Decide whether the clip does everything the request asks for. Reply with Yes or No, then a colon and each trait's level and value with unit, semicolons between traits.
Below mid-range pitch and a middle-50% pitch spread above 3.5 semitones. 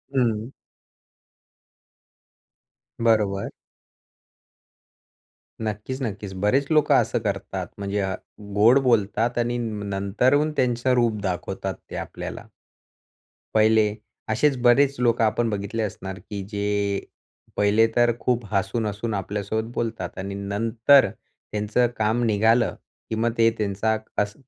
No: low, 110 Hz; narrow, 2.6 semitones